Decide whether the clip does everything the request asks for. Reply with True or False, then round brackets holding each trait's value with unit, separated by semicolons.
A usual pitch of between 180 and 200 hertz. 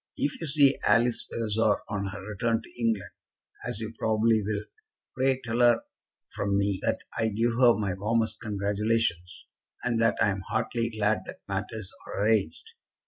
False (110 Hz)